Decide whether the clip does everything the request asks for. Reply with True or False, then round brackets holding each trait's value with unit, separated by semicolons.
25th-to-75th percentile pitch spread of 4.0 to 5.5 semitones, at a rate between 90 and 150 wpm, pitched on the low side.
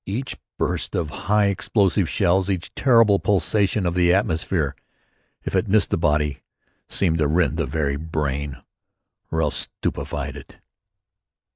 True (4.5 semitones; 140 wpm; 90 Hz)